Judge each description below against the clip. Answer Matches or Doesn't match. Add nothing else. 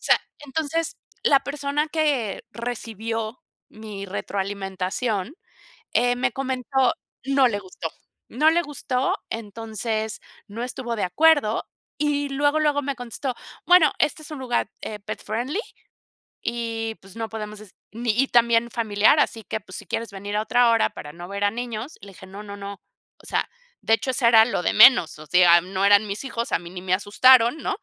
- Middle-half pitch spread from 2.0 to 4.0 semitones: Doesn't match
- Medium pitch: Doesn't match